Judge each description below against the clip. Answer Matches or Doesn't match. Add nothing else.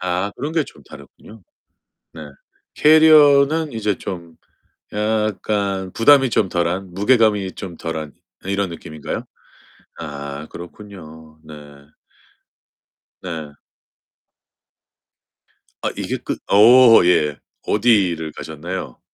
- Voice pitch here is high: Doesn't match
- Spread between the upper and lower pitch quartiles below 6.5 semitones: Matches